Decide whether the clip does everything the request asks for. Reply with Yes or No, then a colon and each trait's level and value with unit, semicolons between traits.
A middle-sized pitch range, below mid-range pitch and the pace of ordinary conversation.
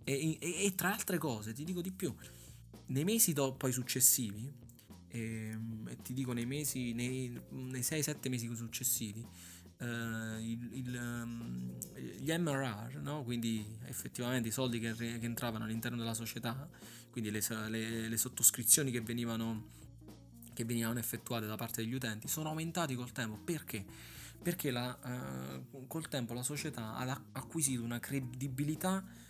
Yes: average, 3.2 semitones; low, 120 Hz; average, 145 wpm